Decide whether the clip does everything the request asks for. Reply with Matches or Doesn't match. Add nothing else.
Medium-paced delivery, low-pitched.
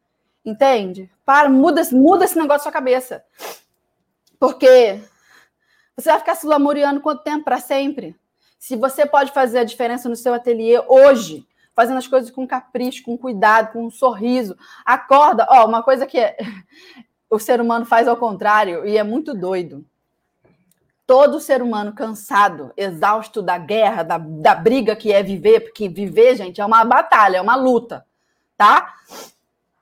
Doesn't match